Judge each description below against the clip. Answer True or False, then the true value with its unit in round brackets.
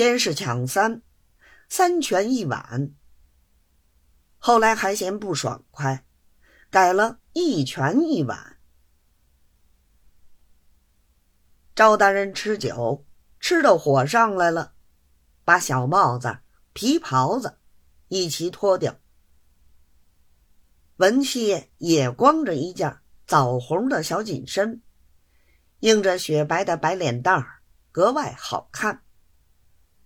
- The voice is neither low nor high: False (130 Hz)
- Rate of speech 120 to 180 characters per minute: True (135 characters per minute)